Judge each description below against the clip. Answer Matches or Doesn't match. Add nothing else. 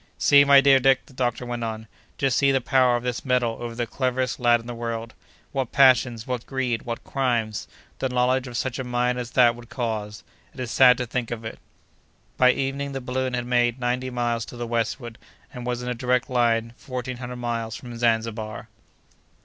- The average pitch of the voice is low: Matches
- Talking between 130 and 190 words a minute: Doesn't match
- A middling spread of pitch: Doesn't match